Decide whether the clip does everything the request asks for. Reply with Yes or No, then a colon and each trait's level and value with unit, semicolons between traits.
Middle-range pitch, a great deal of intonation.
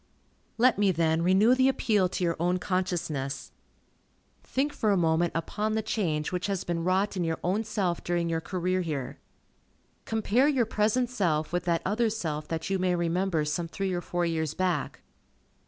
No: medium, 180 Hz; average, 3.9 semitones